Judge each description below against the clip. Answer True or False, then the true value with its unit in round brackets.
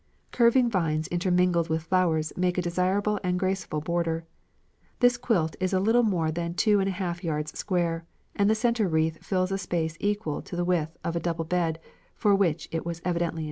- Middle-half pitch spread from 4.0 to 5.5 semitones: False (3.0 semitones)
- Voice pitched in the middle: True (175 Hz)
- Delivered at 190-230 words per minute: True (200 wpm)